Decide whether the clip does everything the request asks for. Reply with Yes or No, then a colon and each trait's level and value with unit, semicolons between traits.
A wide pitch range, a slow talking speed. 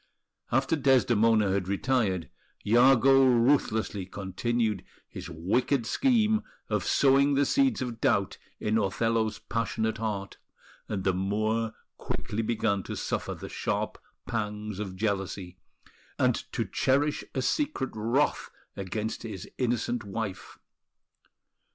No: average, 4.4 semitones; slow, 115 wpm